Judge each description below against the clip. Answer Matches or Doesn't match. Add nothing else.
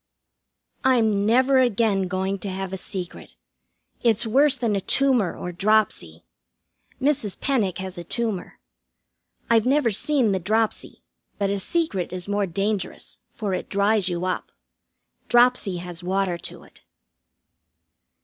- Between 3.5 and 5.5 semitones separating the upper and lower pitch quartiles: Matches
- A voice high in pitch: Matches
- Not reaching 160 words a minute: Matches